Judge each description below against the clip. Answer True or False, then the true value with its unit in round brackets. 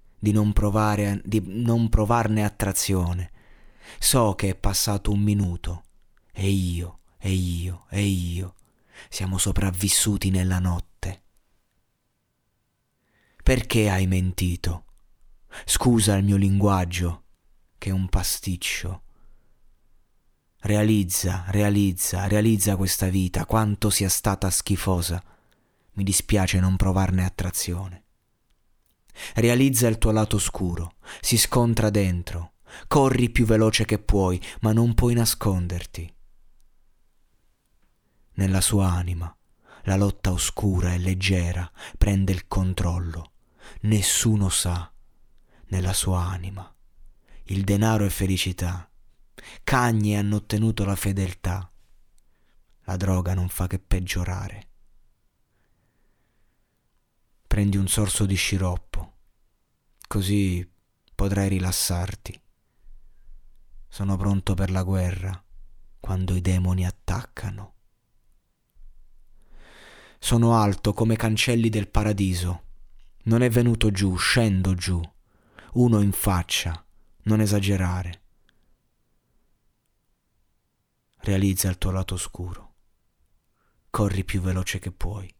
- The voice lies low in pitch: True (95 Hz)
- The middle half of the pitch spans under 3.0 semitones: True (2.6 semitones)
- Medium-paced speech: False (100 wpm)